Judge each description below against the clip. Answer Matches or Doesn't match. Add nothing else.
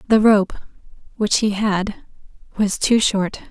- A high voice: Matches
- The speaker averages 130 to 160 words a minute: Matches